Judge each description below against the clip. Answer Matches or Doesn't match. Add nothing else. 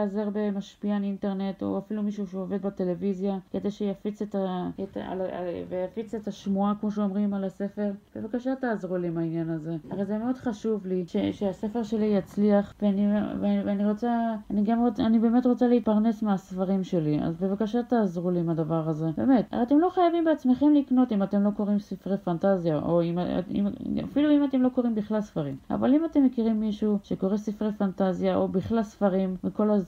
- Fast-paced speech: Matches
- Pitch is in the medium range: Doesn't match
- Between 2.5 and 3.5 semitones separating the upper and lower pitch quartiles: Matches